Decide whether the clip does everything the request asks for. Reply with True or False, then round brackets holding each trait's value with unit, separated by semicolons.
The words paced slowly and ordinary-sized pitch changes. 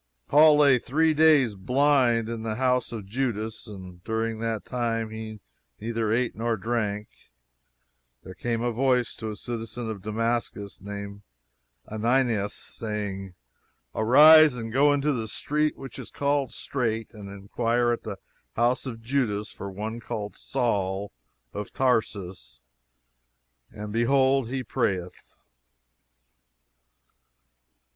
True (125 wpm; 3.3 semitones)